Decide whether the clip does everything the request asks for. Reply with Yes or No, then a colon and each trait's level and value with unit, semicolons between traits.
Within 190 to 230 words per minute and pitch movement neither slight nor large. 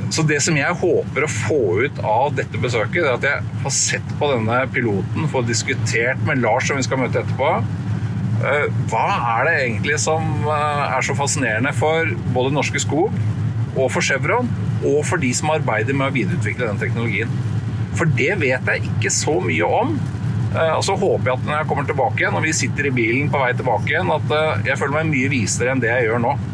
Yes: average, 200 wpm; average, 3.9 semitones